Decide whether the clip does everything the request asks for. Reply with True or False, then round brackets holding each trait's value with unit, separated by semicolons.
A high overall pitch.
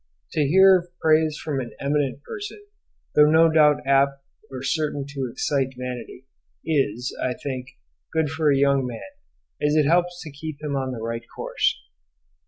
False (145 Hz)